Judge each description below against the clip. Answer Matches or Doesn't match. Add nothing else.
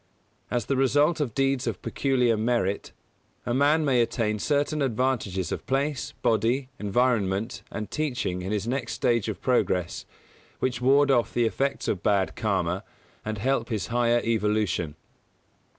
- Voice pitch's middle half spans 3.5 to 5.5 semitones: Matches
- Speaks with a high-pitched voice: Doesn't match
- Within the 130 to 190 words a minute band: Matches